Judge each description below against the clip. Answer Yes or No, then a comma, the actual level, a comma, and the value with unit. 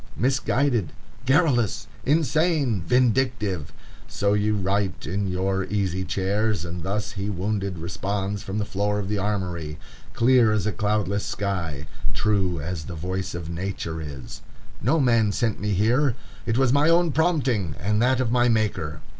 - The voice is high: No, low, 105 Hz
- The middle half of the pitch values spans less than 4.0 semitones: No, average, 4.6 semitones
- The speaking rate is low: No, average, 155 wpm